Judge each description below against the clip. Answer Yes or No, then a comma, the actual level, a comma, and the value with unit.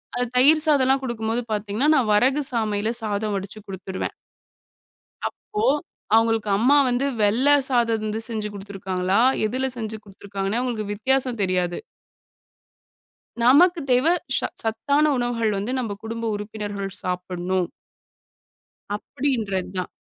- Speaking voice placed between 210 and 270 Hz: Yes, high, 220 Hz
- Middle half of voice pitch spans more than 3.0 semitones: Yes, average, 3.8 semitones